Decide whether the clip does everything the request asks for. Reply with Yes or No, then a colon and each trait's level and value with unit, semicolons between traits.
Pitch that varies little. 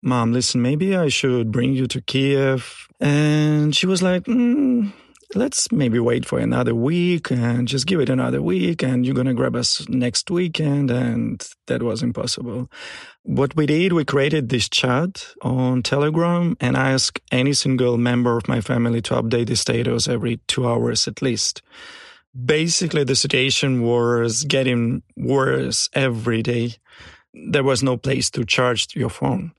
No: average, 3.7 semitones